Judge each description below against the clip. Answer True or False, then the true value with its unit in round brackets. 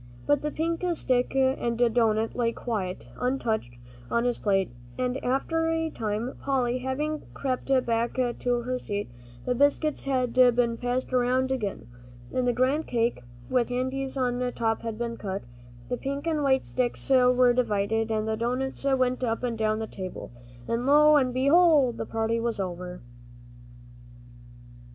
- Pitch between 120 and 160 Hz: False (245 Hz)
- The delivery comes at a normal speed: True (160 wpm)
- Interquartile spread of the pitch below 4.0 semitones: True (2.6 semitones)